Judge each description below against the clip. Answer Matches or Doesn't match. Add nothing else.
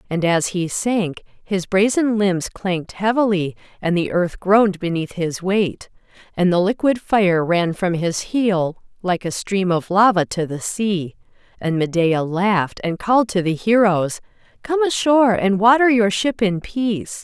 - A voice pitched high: Matches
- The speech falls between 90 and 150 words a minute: Doesn't match